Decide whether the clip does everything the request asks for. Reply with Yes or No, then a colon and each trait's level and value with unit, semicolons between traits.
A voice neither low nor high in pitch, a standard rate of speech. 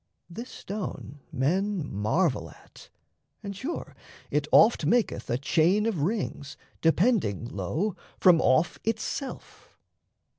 No: medium, 175 Hz; slow, 110 wpm